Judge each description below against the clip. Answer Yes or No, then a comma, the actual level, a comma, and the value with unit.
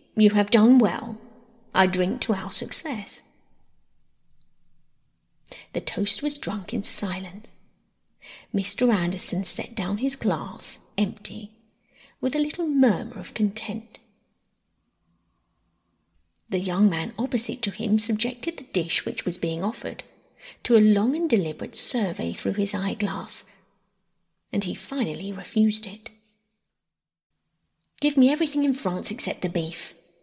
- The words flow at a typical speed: No, slow, 125 wpm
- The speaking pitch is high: Yes, high, 210 Hz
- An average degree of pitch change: Yes, average, 3.8 semitones